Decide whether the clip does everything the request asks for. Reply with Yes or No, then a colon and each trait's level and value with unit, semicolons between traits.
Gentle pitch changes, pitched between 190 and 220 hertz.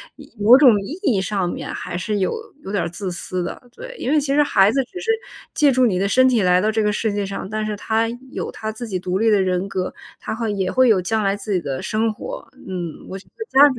No: average, 4.1 semitones; high, 210 Hz